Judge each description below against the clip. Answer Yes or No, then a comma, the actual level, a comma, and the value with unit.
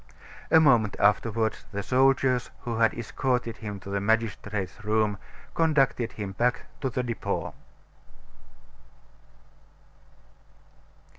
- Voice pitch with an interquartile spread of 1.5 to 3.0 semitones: No, average, 3.4 semitones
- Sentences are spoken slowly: Yes, slow, 100 wpm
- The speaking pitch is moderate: No, low, 115 Hz